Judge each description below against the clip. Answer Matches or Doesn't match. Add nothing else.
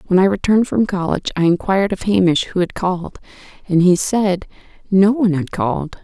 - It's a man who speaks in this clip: Doesn't match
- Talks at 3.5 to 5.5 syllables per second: Doesn't match